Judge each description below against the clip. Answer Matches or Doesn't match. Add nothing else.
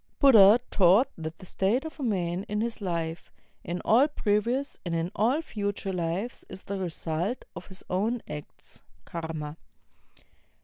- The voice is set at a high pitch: Matches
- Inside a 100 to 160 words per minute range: Matches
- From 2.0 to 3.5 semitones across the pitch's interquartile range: Doesn't match